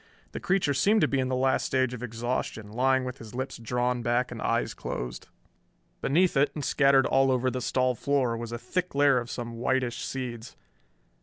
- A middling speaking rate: Yes, average, 190 wpm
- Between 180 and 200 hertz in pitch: No, low, 130 Hz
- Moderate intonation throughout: No, narrow, 2.2 semitones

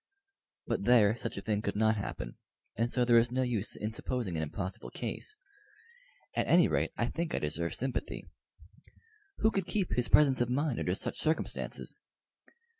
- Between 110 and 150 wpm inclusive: No, average, 175 wpm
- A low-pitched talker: Yes, low, 120 Hz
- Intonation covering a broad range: No, average, 4.0 semitones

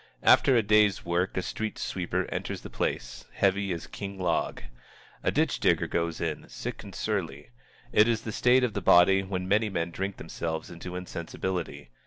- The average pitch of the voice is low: Yes, very low, 95 Hz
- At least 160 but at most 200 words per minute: Yes, average, 180 wpm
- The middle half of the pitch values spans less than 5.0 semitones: Yes, average, 3.3 semitones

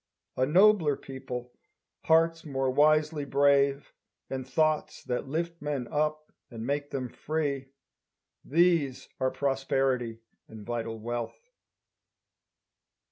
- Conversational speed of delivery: No, slow, 105 wpm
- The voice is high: No, medium, 140 Hz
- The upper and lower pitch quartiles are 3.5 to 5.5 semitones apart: No, average, 3.1 semitones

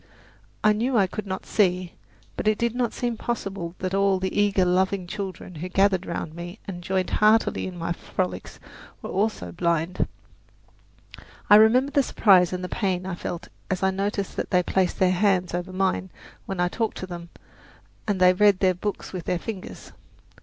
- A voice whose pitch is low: No, high, 190 Hz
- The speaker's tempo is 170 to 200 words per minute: Yes, average, 185 wpm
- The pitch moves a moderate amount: No, narrow, 2.3 semitones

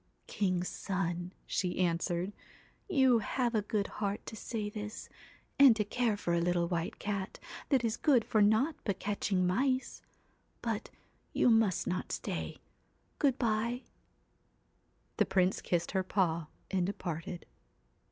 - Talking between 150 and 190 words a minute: No, average, 140 wpm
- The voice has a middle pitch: No, high, 205 Hz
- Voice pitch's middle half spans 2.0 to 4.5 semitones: Yes, average, 3.9 semitones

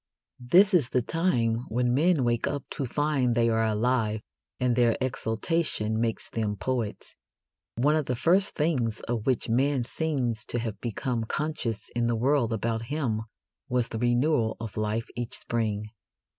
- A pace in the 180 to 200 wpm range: No, average, 160 wpm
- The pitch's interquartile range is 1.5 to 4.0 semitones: Yes, average, 3.5 semitones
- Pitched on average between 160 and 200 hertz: No, low, 120 Hz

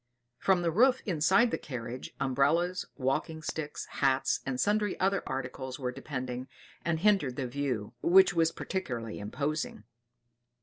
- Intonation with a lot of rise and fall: Yes, wide, 5.8 semitones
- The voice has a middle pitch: Yes, medium, 145 Hz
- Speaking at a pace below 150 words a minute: Yes, slow, 135 wpm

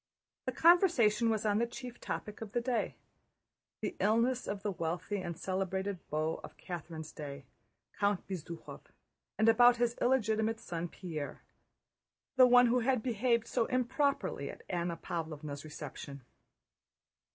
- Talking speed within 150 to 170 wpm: No, average, 140 wpm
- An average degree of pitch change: No, wide, 5.9 semitones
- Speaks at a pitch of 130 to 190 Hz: No, high, 210 Hz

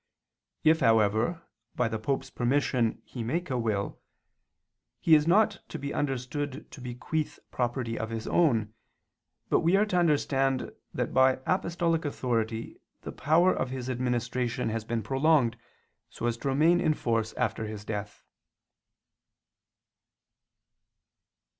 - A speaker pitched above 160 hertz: No, low, 130 Hz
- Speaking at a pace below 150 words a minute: Yes, slow, 135 wpm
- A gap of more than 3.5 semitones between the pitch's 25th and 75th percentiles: Yes, average, 5.3 semitones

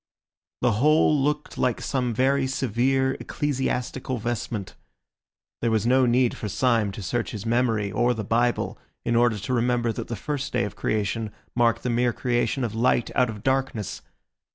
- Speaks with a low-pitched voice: Yes, low, 120 Hz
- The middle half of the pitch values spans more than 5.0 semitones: No, narrow, 2.6 semitones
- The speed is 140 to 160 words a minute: No, average, 170 wpm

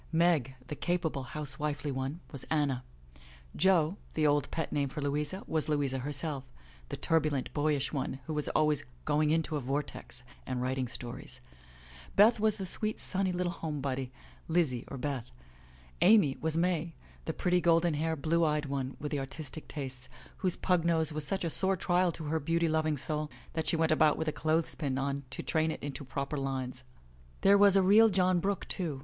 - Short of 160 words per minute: No, average, 190 wpm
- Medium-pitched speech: Yes, medium, 155 Hz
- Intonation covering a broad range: No, average, 3.5 semitones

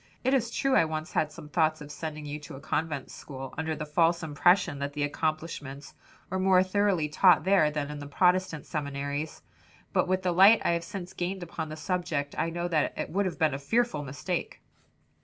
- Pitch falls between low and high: Yes, medium, 160 Hz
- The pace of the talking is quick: Yes, fast, 210 wpm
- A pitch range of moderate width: Yes, average, 3.6 semitones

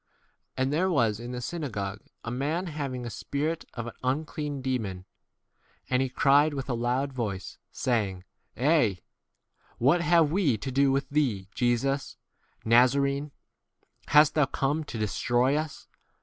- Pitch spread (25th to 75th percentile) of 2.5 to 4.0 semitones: Yes, average, 3.7 semitones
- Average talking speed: Yes, average, 165 wpm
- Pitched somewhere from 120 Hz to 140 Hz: Yes, low, 135 Hz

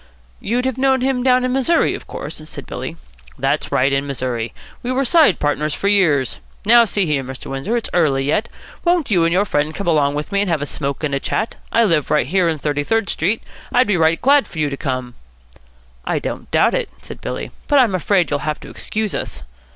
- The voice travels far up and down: Yes, wide, 8.3 semitones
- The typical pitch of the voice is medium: Yes, medium, 170 Hz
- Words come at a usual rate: No, fast, 230 wpm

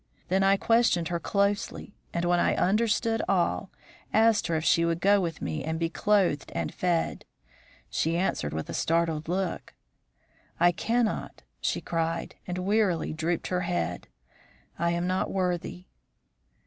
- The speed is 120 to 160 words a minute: Yes, average, 150 wpm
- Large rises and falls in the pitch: No, average, 3.1 semitones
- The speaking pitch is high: No, medium, 175 Hz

